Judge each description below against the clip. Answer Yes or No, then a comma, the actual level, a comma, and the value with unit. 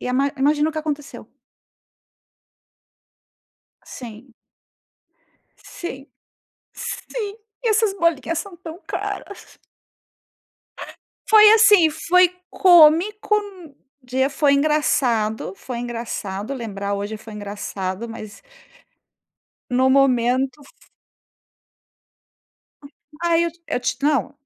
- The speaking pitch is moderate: No, very high, 275 Hz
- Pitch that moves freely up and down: Yes, wide, 6.2 semitones